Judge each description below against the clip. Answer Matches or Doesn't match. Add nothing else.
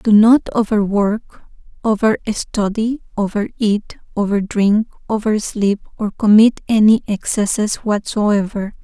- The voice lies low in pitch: Doesn't match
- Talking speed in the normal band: Doesn't match